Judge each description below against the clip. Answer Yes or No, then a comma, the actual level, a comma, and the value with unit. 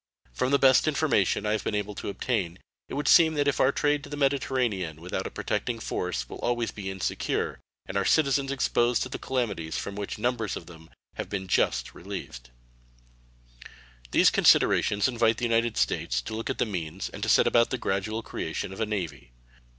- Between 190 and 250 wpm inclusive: Yes, average, 200 wpm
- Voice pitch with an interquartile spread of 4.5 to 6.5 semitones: Yes, average, 5.3 semitones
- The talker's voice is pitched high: No, low, 110 Hz